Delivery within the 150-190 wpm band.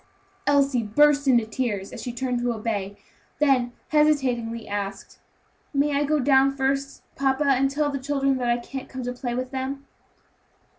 Yes: average, 165 wpm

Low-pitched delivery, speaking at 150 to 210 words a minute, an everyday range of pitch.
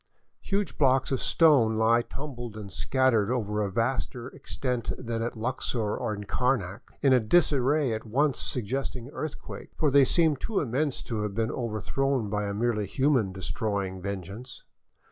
Yes: low, 120 Hz; average, 160 wpm; average, 4.1 semitones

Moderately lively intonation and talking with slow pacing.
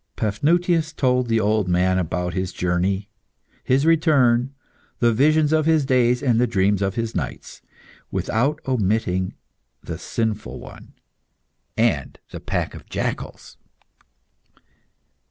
No: wide, 6.2 semitones; slow, 120 wpm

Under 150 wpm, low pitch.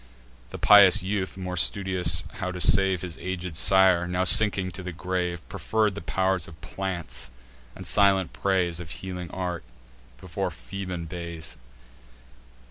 Yes: average, 140 wpm; very low, 90 Hz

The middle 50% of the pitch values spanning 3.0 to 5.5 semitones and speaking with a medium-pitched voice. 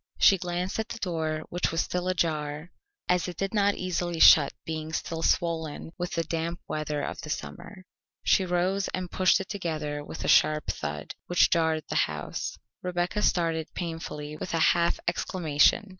No: narrow, 2.4 semitones; medium, 170 Hz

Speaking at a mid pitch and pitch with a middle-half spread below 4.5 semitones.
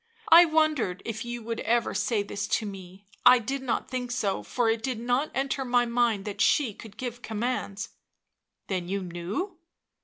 No: high, 235 Hz; average, 4.0 semitones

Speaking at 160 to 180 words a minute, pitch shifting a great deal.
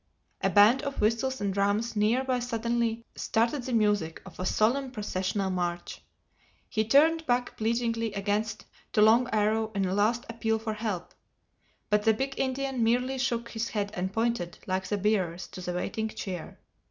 No: average, 170 wpm; average, 2.9 semitones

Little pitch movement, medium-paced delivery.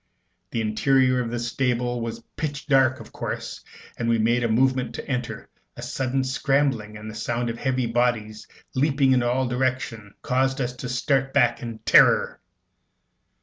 Yes: narrow, 2.2 semitones; average, 165 wpm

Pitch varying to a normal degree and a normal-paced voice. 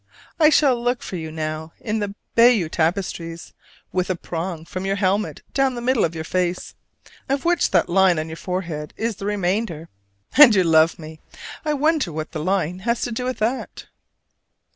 No: wide, 6.1 semitones; average, 185 wpm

